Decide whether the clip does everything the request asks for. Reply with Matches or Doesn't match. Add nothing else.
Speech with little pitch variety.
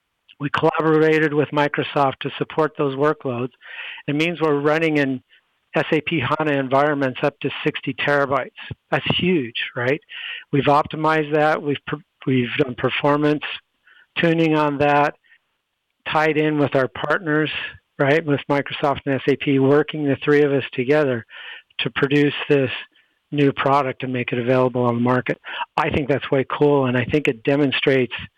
Matches